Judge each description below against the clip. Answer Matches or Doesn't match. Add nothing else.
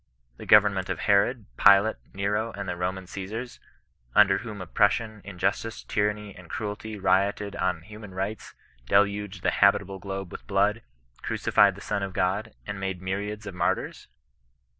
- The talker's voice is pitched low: Matches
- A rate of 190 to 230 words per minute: Doesn't match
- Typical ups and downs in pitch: Doesn't match